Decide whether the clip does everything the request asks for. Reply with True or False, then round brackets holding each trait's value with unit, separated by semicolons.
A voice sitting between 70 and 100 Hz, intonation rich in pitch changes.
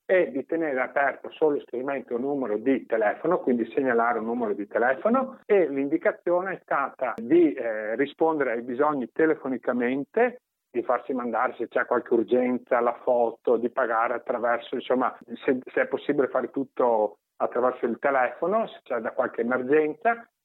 False (140 Hz; 5.7 semitones)